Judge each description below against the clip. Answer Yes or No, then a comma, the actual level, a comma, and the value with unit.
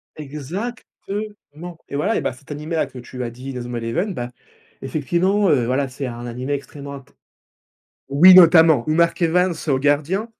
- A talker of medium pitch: Yes, medium, 145 Hz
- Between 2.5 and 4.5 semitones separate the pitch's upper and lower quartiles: No, average, 4.9 semitones